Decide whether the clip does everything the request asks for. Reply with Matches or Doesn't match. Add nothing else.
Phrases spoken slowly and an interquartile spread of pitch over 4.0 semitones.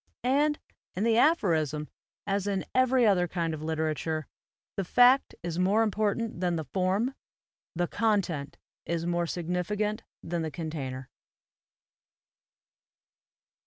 Matches